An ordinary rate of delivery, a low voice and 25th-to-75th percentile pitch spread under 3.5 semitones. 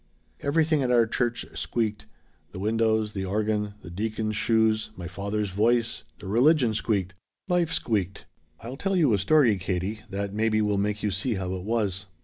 Yes: average, 170 wpm; low, 110 Hz; average, 2.8 semitones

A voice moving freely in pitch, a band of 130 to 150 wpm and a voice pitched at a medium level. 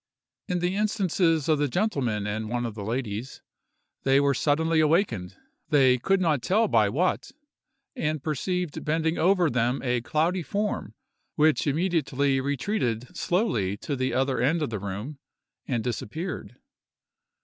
Yes: wide, 5.9 semitones; average, 145 wpm; medium, 145 Hz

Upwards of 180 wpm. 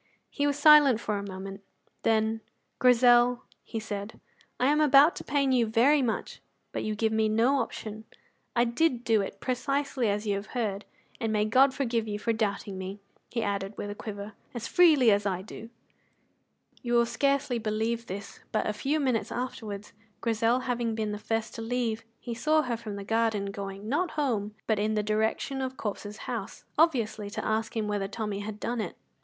Yes: average, 190 wpm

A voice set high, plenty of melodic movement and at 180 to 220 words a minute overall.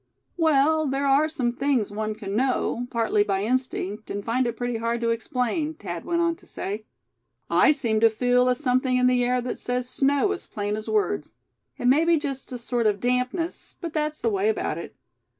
No: very high, 250 Hz; average, 4.0 semitones; fast, 205 wpm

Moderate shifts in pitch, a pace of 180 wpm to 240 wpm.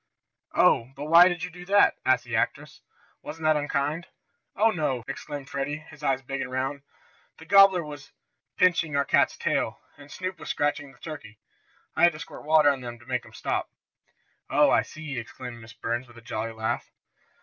Yes: average, 4.2 semitones; average, 195 wpm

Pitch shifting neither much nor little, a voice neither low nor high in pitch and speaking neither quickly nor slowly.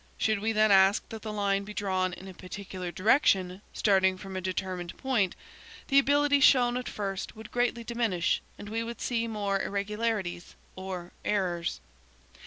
No: average, 3.4 semitones; high, 200 Hz; average, 170 wpm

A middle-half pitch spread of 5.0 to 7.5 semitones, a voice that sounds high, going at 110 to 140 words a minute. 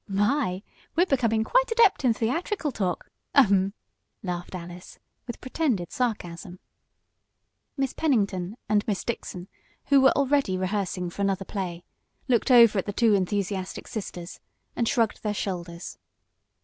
Yes: wide, 5.4 semitones; high, 205 Hz; slow, 135 wpm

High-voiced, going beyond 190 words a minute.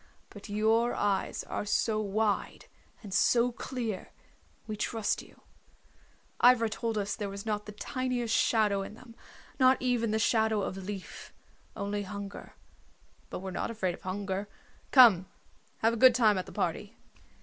No: high, 215 Hz; average, 155 wpm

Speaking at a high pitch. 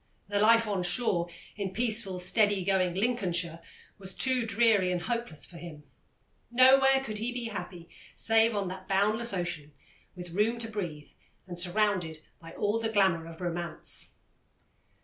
Yes: high, 195 Hz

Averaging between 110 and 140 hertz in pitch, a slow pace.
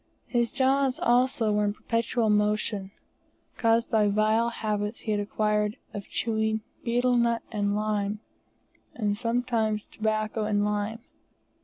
No: high, 215 Hz; slow, 130 wpm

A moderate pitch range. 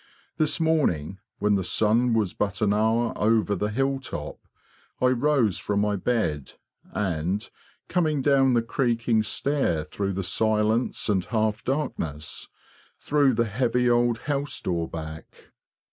Yes: average, 4.3 semitones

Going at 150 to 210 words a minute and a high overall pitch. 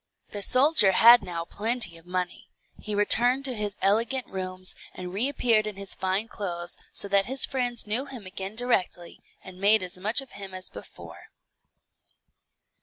Yes: average, 165 wpm; high, 205 Hz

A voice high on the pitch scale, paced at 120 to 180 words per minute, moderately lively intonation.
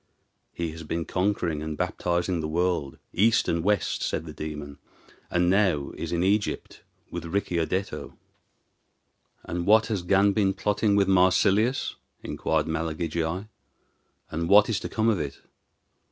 No: very low, 90 Hz; average, 140 wpm; average, 3.7 semitones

